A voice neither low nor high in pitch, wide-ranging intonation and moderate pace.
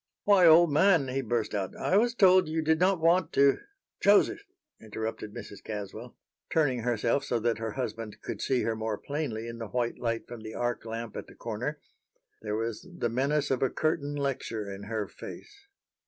No: low, 120 Hz; wide, 5.9 semitones; average, 190 wpm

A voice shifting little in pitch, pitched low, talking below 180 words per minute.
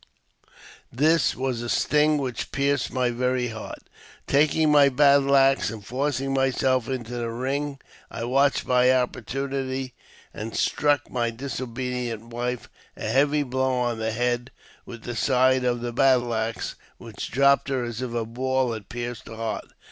Yes: narrow, 2.3 semitones; low, 125 Hz; average, 155 wpm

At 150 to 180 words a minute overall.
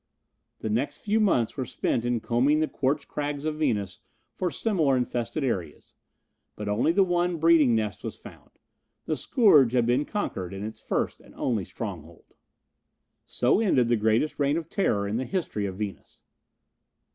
Yes: average, 170 wpm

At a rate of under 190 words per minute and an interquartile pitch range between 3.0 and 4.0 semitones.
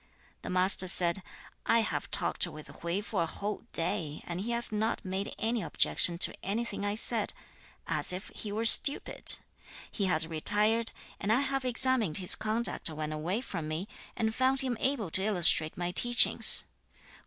No: average, 170 wpm; average, 4.8 semitones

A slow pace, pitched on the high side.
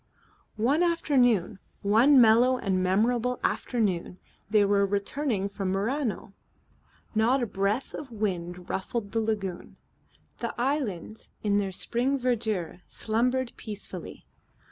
Yes: slow, 115 wpm; high, 220 Hz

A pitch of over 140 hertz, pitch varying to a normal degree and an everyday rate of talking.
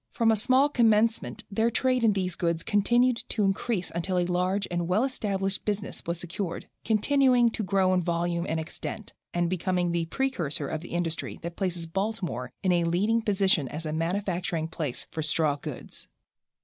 Yes: medium, 185 Hz; average, 4.1 semitones; average, 175 wpm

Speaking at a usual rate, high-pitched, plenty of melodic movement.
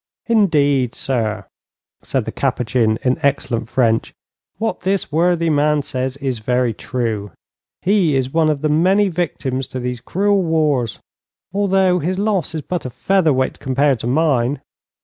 No: average, 150 wpm; medium, 140 Hz; wide, 5.7 semitones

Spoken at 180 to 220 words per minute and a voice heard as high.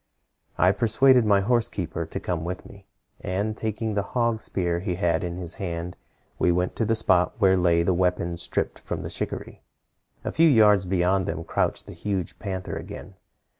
No: average, 185 wpm; very low, 95 Hz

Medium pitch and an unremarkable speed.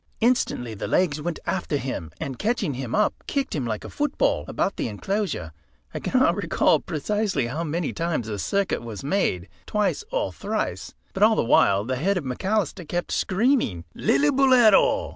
Yes: medium, 170 Hz; average, 170 wpm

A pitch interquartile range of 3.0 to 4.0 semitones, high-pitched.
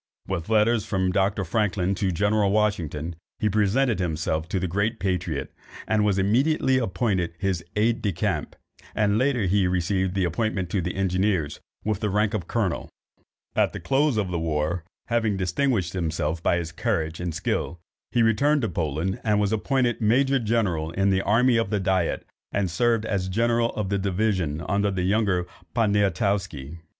No: average, 3.6 semitones; low, 100 Hz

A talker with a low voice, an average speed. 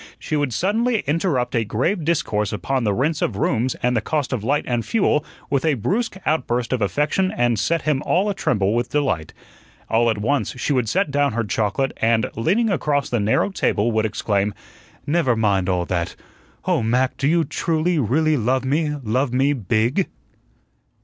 Yes: low, 130 Hz; average, 185 wpm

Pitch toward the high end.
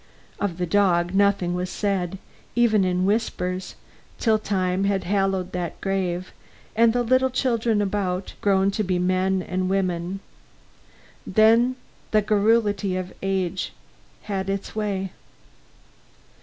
Yes: high, 195 Hz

